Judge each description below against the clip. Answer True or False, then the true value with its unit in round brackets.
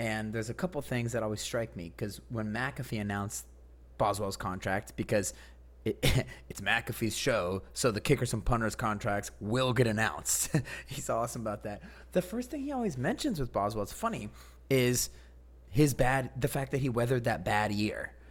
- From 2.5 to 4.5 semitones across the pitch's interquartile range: True (4.2 semitones)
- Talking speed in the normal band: True (175 wpm)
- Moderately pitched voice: False (110 Hz)